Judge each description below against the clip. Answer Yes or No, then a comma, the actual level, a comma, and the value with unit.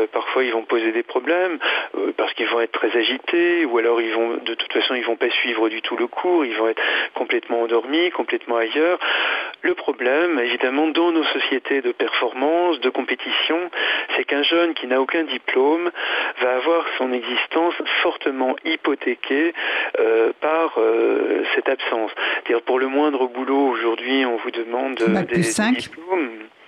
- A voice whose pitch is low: No, medium, 160 Hz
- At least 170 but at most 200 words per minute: Yes, average, 175 wpm